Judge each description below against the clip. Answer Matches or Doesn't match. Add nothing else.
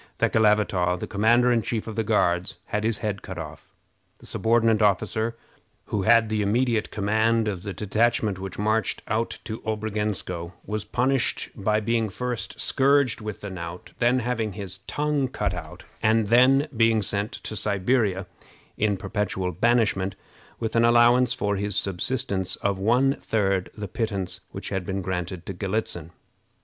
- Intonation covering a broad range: Doesn't match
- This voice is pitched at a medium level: Doesn't match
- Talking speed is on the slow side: Doesn't match